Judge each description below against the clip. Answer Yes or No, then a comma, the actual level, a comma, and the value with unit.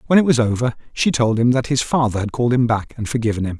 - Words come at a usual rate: No, fast, 285 wpm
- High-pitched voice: No, low, 120 Hz